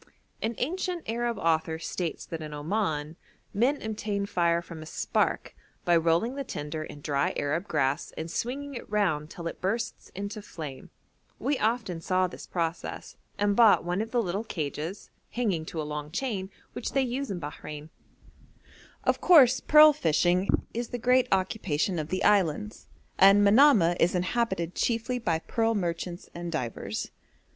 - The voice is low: No, medium, 185 Hz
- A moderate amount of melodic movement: No, wide, 6.0 semitones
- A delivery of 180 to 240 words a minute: No, average, 160 wpm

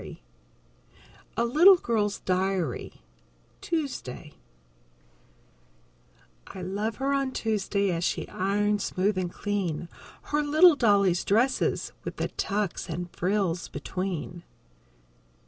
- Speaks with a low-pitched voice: No, high, 200 Hz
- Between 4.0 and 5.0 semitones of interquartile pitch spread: Yes, average, 4.4 semitones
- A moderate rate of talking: No, slow, 105 wpm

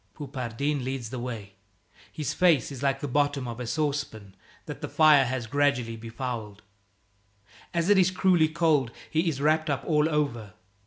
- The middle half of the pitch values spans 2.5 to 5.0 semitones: Yes, average, 4.5 semitones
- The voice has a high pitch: No, medium, 140 Hz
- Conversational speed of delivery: Yes, average, 165 wpm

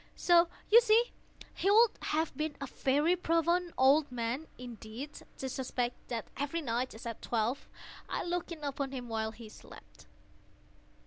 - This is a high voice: Yes, very high, 275 Hz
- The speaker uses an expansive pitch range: Yes, wide, 5.7 semitones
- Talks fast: No, average, 155 wpm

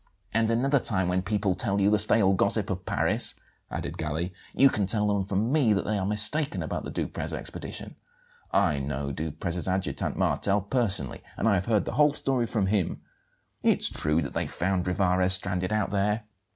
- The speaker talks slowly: No, average, 185 wpm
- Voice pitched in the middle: No, low, 100 Hz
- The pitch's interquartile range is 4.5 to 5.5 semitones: No, average, 3.0 semitones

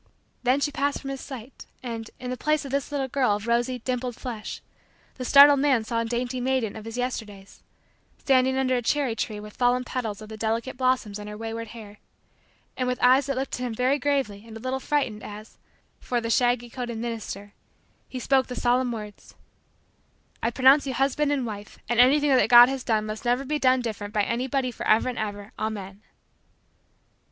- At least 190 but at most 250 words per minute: Yes, average, 200 wpm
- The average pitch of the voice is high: Yes, high, 245 Hz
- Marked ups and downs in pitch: No, average, 3.1 semitones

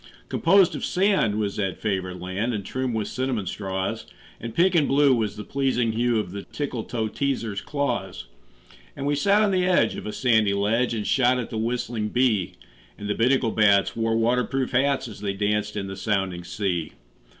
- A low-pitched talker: Yes, low, 115 Hz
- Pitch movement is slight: No, average, 4.3 semitones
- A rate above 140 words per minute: Yes, average, 190 wpm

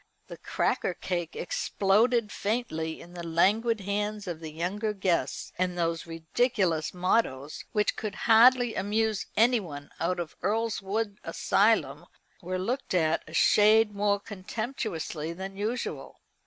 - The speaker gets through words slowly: Yes, slow, 130 wpm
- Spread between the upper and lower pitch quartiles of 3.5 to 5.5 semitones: Yes, average, 4.3 semitones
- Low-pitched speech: No, high, 200 Hz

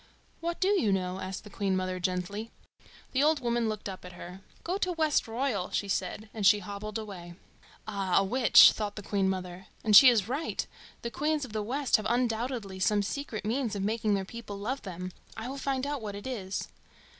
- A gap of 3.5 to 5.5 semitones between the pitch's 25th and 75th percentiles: Yes, average, 4.7 semitones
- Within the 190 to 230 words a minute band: Yes, fast, 205 wpm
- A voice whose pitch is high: Yes, high, 215 Hz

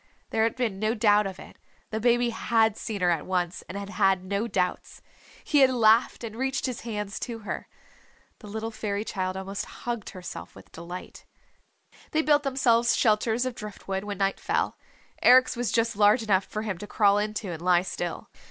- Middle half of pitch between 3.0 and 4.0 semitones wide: Yes, average, 3.3 semitones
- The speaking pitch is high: Yes, high, 215 Hz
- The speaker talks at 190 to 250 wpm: Yes, average, 195 wpm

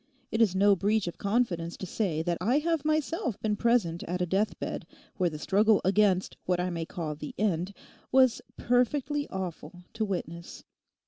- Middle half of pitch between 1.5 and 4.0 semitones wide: No, average, 4.9 semitones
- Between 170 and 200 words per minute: Yes, average, 180 wpm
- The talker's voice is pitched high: Yes, high, 195 Hz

